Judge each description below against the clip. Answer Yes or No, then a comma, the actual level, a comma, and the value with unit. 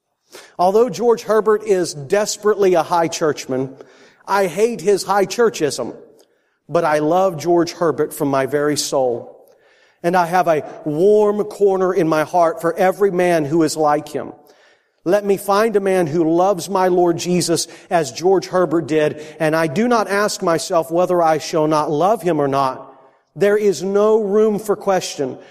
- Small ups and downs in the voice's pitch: No, average, 4.3 semitones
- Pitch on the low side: No, medium, 180 Hz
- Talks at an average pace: Yes, average, 170 wpm